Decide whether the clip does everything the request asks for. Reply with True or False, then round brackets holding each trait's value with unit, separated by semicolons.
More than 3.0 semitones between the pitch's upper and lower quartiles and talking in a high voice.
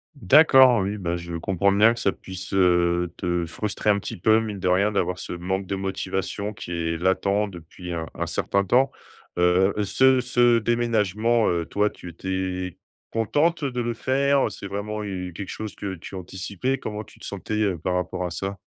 False (3.4 semitones; 100 Hz)